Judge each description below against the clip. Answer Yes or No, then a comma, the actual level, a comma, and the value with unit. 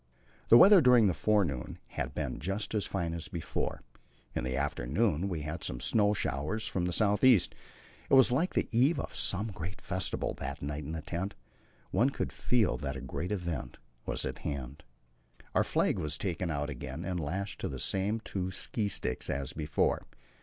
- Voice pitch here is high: No, very low, 90 Hz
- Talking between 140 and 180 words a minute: No, average, 190 wpm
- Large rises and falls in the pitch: Yes, wide, 6.1 semitones